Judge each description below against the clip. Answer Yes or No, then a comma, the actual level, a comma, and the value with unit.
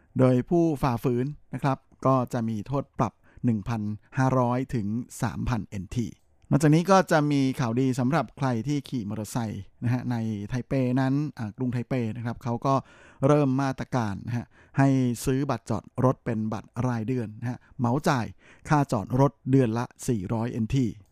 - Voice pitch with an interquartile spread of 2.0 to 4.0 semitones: Yes, average, 2.9 semitones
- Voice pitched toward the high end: No, low, 125 Hz